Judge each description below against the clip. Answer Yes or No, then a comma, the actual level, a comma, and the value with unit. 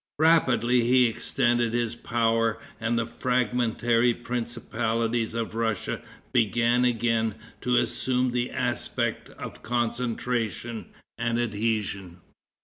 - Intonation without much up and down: Yes, narrow, 1.3 semitones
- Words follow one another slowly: Yes, slow, 100 wpm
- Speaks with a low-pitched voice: Yes, low, 120 Hz